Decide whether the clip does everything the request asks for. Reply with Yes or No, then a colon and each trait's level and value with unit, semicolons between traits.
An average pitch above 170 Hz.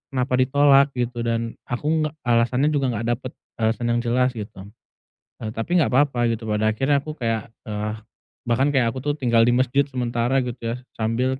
No: low, 120 Hz